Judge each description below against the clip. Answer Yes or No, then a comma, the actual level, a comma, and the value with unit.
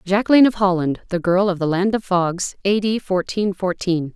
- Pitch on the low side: No, high, 190 Hz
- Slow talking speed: No, average, 200 wpm